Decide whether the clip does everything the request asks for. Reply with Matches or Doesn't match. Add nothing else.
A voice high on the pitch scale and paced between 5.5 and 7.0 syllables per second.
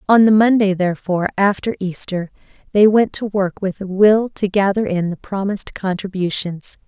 Doesn't match